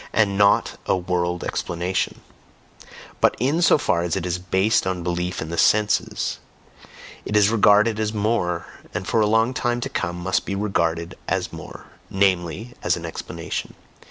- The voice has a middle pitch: No, very low, 95 Hz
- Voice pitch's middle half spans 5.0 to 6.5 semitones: No, average, 3.6 semitones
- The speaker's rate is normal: Yes, average, 165 wpm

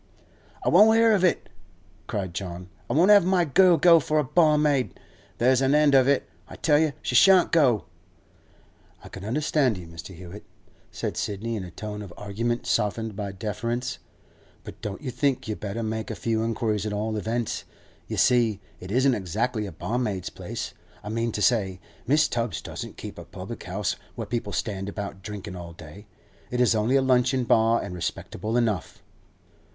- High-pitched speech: No, low, 115 Hz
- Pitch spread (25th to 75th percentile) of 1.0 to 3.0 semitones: No, average, 4.7 semitones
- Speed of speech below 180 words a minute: No, average, 185 wpm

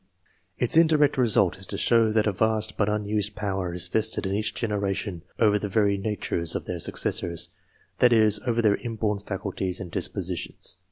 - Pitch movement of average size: No, narrow, 2.3 semitones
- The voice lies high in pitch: No, low, 105 Hz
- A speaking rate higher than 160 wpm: Yes, average, 175 wpm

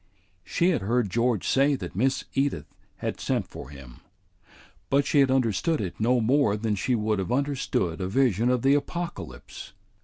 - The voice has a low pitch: Yes, low, 120 Hz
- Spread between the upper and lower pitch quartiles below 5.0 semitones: No, wide, 5.4 semitones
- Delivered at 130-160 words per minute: No, average, 175 wpm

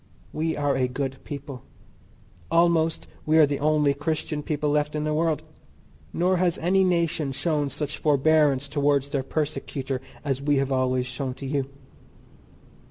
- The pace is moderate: Yes, average, 155 wpm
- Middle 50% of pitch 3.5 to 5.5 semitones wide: No, narrow, 2.4 semitones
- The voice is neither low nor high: Yes, medium, 145 Hz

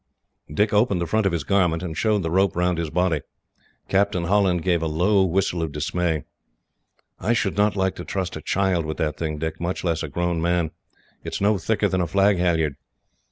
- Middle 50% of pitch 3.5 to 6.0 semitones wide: No, average, 3.1 semitones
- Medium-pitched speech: No, very low, 90 Hz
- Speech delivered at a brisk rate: Yes, fast, 210 wpm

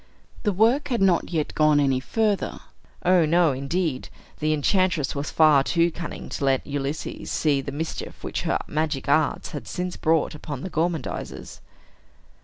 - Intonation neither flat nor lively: Yes, average, 3.7 semitones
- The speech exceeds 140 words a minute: Yes, average, 160 wpm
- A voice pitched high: No, medium, 155 Hz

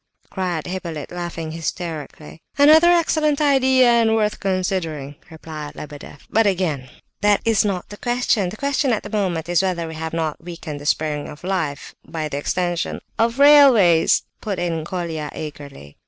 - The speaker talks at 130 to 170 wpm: Yes, average, 160 wpm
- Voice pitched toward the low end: No, medium, 175 Hz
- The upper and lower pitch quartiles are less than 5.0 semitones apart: No, wide, 5.5 semitones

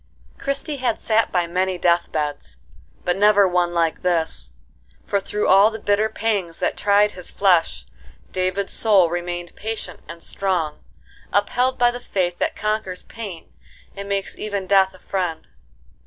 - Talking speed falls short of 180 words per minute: Yes, average, 155 wpm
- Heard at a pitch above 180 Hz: Yes, high, 190 Hz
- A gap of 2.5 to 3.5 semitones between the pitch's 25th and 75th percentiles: Yes, average, 3.1 semitones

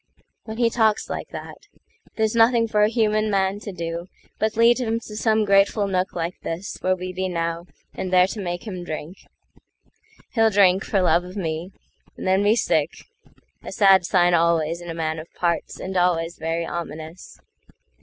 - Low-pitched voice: No, medium, 185 Hz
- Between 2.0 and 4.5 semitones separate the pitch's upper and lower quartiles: Yes, average, 3.8 semitones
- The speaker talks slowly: No, average, 165 wpm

